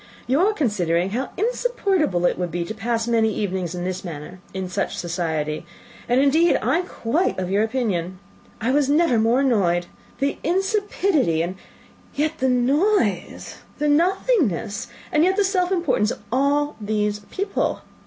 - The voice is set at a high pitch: Yes, high, 240 Hz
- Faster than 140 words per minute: Yes, average, 160 wpm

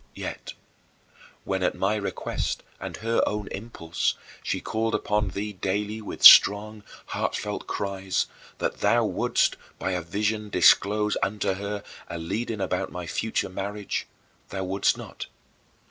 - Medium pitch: No, low, 100 Hz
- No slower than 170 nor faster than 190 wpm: No, slow, 135 wpm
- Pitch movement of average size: No, narrow, 1.8 semitones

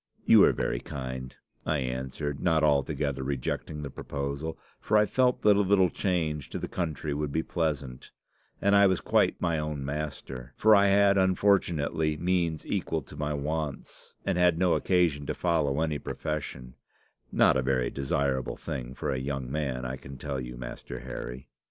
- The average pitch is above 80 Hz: No, very low, 75 Hz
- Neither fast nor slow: Yes, average, 175 wpm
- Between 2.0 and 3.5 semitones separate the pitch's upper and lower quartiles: No, average, 4.2 semitones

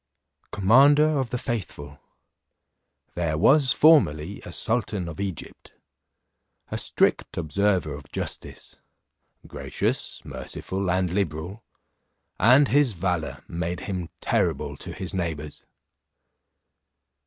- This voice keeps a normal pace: No, slow, 100 wpm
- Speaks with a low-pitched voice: Yes, very low, 95 Hz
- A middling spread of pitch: No, wide, 6.1 semitones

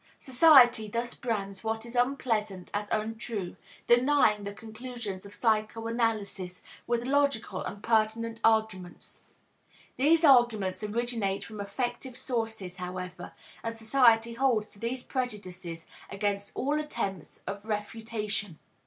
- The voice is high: Yes, high, 225 Hz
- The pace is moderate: No, slow, 115 wpm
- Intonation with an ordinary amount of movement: Yes, average, 3.1 semitones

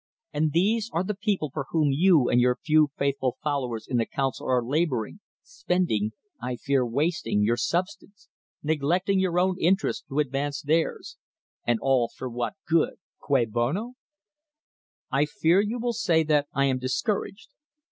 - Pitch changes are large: Yes, wide, 5.8 semitones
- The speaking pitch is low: No, medium, 150 Hz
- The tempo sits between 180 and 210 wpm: No, average, 165 wpm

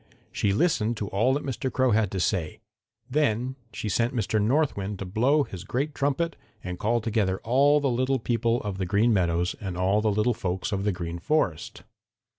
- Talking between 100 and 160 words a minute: No, average, 200 wpm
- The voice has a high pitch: No, low, 110 Hz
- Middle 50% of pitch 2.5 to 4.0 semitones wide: No, average, 5.1 semitones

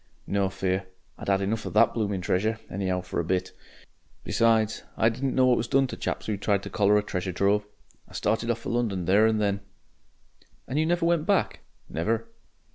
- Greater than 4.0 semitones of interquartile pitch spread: No, average, 3.0 semitones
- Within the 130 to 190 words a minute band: No, average, 200 wpm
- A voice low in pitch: Yes, low, 105 Hz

